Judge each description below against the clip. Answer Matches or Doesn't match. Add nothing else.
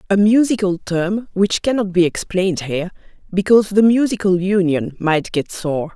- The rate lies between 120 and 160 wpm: Matches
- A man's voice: Doesn't match